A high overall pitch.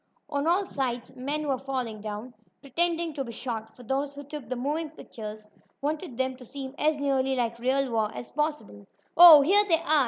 Yes: very high, 270 Hz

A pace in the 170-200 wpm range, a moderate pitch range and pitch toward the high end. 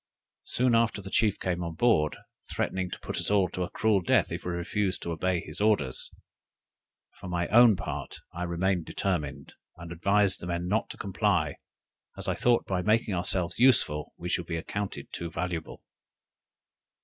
No: average, 175 wpm; average, 3.2 semitones; very low, 90 Hz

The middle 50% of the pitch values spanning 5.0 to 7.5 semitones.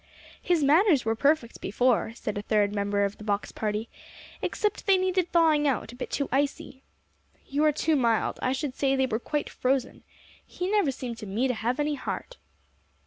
Yes: average, 5.3 semitones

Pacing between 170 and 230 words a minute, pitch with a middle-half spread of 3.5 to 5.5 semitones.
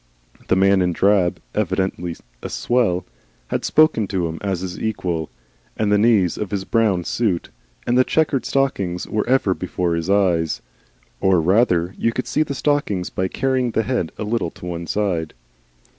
Yes: average, 175 wpm; average, 4.5 semitones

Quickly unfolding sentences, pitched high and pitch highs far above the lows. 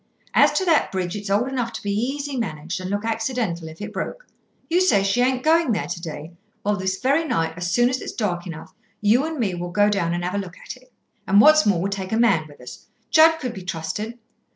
Yes: fast, 245 wpm; high, 205 Hz; wide, 6.1 semitones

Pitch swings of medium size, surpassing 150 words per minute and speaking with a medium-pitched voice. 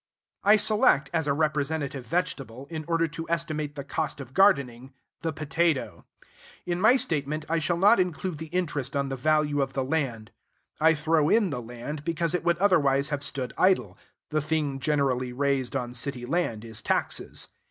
Yes: average, 3.5 semitones; average, 175 wpm; medium, 150 Hz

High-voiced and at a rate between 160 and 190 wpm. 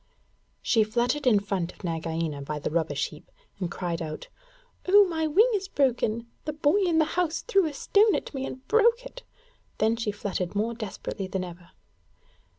Yes: high, 230 Hz; average, 180 wpm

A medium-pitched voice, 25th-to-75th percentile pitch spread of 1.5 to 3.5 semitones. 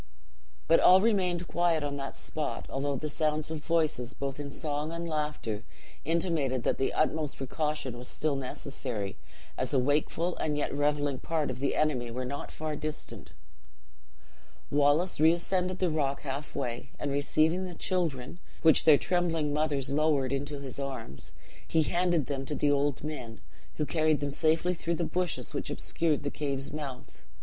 Yes: medium, 150 Hz; average, 2.7 semitones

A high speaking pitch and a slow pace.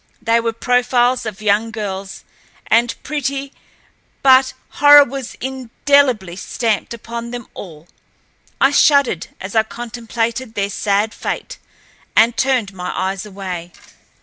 Yes: high, 230 Hz; slow, 120 wpm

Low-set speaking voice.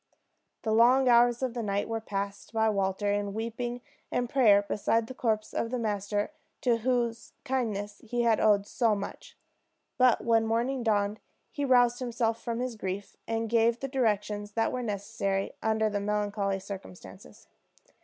No: high, 225 Hz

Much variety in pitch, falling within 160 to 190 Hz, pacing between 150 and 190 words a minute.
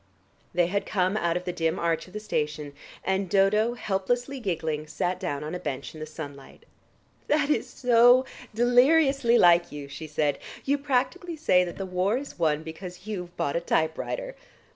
Yes: wide, 7.2 semitones; medium, 185 Hz; average, 175 wpm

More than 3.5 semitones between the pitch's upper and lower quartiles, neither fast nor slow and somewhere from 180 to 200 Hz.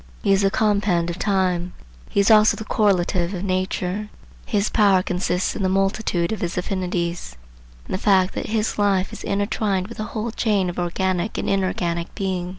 No: narrow, 2.4 semitones; average, 185 wpm; high, 190 Hz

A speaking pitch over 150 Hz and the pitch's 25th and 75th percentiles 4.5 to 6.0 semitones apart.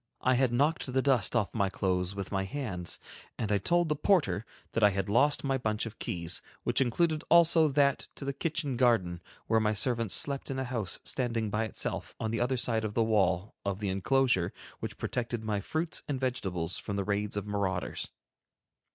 No: low, 115 Hz; average, 5.1 semitones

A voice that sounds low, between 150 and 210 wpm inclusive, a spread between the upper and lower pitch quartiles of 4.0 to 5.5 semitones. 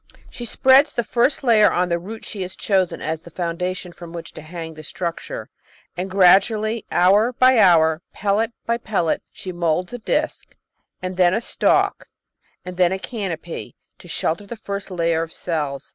No: medium, 185 Hz; average, 180 wpm; average, 4.3 semitones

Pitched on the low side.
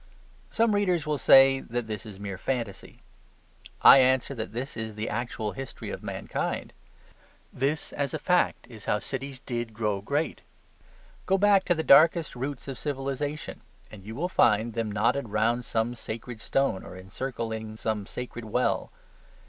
Yes: low, 120 Hz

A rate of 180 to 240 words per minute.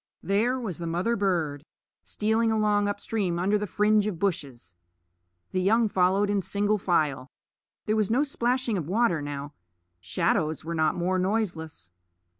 No: average, 155 wpm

